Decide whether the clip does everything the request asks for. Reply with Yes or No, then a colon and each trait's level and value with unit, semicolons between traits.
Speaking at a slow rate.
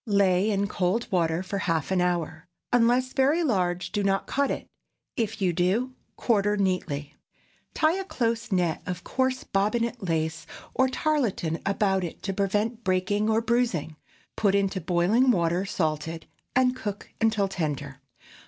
No: average, 150 wpm